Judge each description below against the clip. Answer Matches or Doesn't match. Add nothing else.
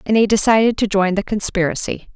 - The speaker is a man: Doesn't match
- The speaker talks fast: Doesn't match